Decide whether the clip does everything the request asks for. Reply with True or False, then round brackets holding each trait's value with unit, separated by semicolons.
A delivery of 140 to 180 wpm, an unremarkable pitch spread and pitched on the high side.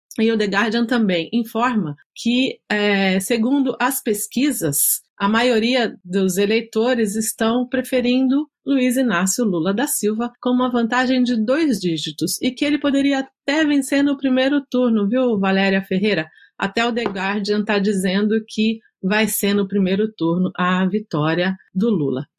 True (150 wpm; 4.4 semitones; 220 Hz)